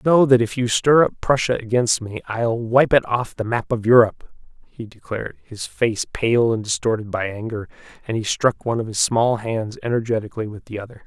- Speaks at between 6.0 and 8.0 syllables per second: No, 5.3 syllables/s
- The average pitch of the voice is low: Yes, low, 115 Hz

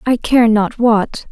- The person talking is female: Yes, female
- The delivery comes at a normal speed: Yes, average, 185 wpm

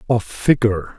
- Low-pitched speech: Yes, low, 115 Hz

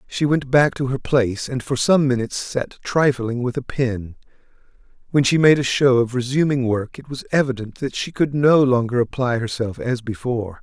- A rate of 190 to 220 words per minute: Yes, average, 200 wpm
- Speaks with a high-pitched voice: No, low, 130 Hz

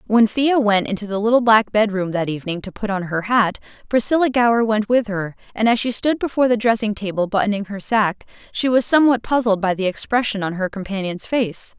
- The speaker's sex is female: Yes, female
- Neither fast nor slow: No, fast, 215 wpm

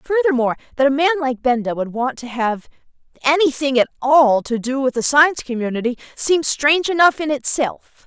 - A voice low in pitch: No, very high, 270 Hz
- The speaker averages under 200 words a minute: Yes, average, 180 wpm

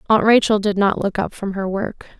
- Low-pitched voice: No, high, 205 Hz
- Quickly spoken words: Yes, fast, 245 wpm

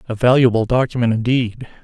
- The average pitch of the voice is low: Yes, low, 120 Hz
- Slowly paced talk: Yes, slow, 130 wpm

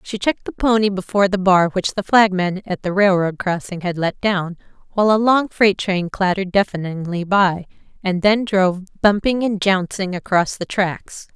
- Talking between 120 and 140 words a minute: No, average, 180 wpm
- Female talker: Yes, female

